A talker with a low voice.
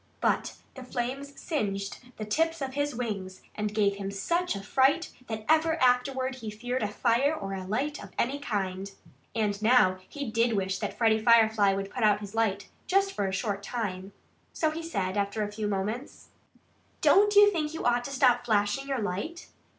No: high, 225 Hz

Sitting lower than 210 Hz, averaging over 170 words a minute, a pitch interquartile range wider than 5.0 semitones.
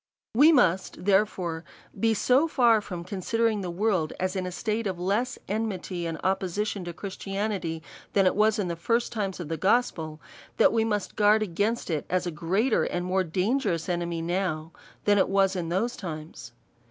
No: high, 190 Hz; average, 185 wpm; average, 3.8 semitones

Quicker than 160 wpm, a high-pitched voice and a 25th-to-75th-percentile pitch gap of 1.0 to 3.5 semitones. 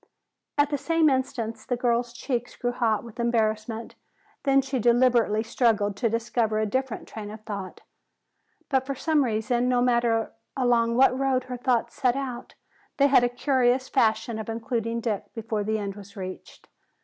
Yes: average, 170 wpm; high, 235 Hz; narrow, 2.6 semitones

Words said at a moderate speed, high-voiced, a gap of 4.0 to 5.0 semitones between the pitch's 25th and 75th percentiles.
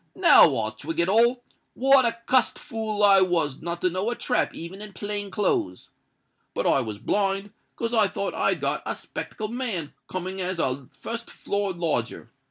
Yes: average, 180 wpm; high, 195 Hz; average, 4.7 semitones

